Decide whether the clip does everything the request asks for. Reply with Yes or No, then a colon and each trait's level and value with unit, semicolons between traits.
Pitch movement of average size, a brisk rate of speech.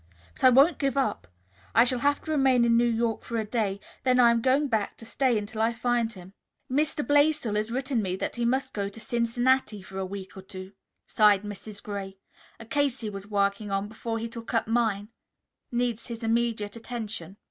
Yes: average, 3.2 semitones; fast, 210 wpm